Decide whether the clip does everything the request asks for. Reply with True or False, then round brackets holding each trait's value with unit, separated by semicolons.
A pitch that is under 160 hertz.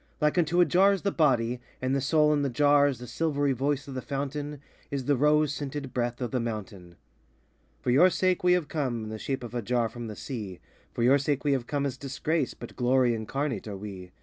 True (135 Hz)